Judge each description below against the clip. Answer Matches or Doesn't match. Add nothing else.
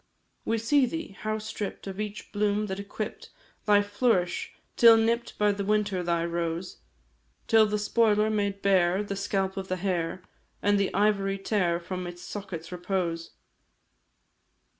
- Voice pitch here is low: Doesn't match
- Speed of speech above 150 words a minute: Doesn't match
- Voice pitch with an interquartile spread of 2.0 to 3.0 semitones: Matches